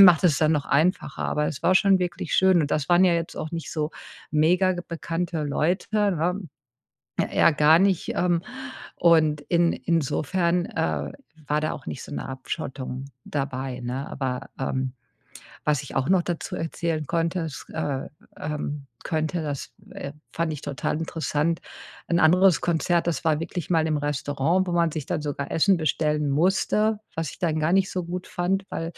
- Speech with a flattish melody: No, average, 3.0 semitones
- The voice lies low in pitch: No, medium, 160 Hz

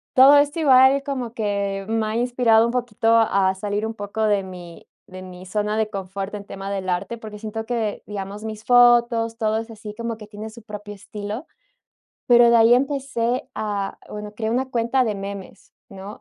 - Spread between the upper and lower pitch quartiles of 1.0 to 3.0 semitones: Yes, narrow, 2.6 semitones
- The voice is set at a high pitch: Yes, high, 220 Hz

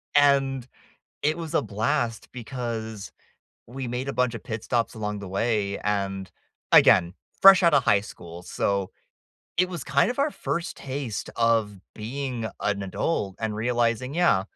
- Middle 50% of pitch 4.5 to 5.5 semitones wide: Yes, average, 4.8 semitones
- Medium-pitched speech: No, low, 115 Hz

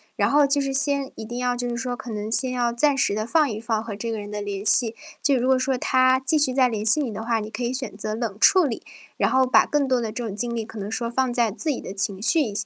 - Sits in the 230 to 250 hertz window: Yes, high, 240 Hz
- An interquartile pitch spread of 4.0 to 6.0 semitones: No, average, 3.3 semitones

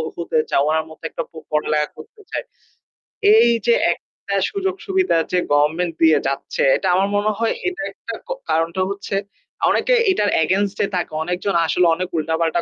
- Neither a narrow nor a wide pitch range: No, wide, 6.2 semitones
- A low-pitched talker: No, medium, 180 Hz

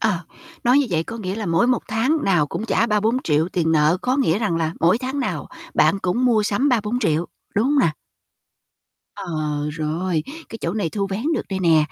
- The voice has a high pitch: Yes, high, 200 Hz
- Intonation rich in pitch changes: Yes, wide, 6.0 semitones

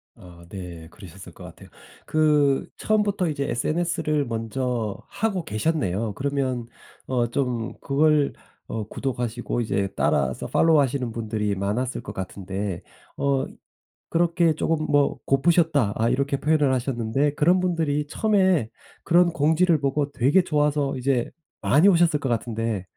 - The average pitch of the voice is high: No, medium, 140 Hz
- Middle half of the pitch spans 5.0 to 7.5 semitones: Yes, wide, 5.6 semitones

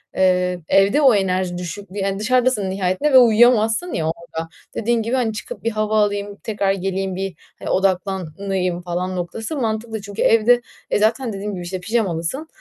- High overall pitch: Yes, high, 200 Hz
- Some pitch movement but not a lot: Yes, average, 3.3 semitones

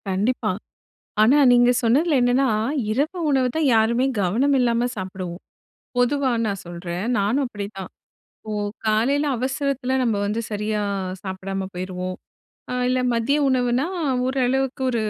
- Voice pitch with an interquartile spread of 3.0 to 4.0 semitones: No, average, 4.7 semitones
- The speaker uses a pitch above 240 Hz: No, high, 235 Hz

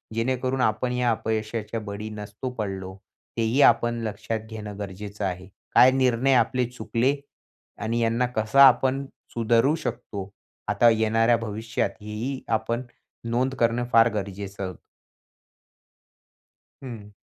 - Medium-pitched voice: No, low, 115 Hz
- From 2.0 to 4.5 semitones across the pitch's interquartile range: Yes, average, 2.7 semitones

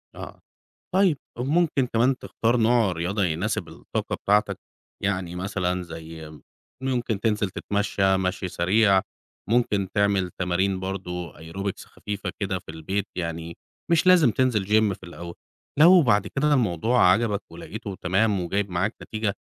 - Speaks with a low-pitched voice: Yes, low, 100 Hz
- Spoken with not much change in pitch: No, average, 3.9 semitones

